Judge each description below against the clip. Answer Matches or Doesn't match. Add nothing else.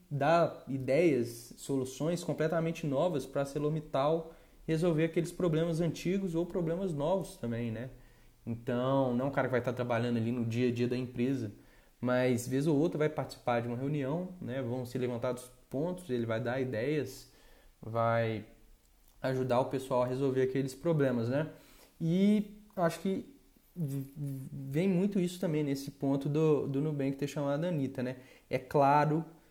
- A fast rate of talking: Doesn't match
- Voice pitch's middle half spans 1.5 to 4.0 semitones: Doesn't match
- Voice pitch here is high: Doesn't match